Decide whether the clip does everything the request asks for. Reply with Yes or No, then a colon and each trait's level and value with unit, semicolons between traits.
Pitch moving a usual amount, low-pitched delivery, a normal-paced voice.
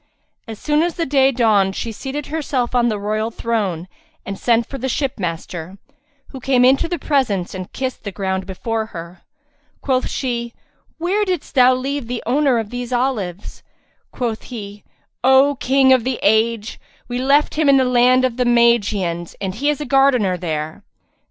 No: average, 4.6 semitones; high, 240 Hz; average, 175 wpm